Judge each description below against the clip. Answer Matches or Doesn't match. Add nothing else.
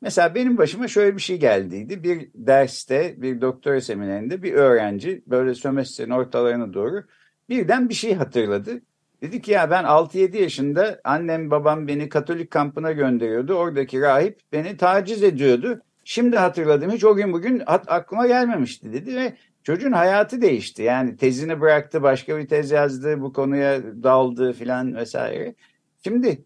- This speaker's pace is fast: Matches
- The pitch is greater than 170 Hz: Doesn't match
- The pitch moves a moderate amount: Doesn't match